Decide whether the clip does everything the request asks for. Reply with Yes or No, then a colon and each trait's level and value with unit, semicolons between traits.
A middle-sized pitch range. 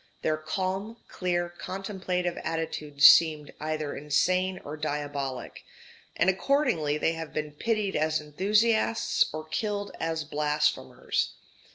Yes: average, 3.9 semitones